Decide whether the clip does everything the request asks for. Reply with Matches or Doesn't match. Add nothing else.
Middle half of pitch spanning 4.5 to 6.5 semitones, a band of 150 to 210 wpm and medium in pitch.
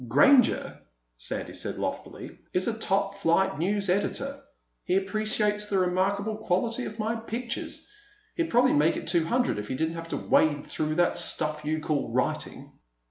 Doesn't match